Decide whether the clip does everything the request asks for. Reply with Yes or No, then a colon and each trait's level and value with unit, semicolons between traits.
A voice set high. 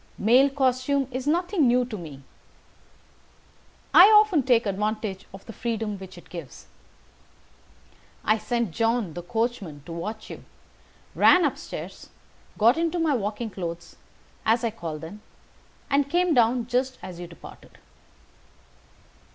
Yes: high, 230 Hz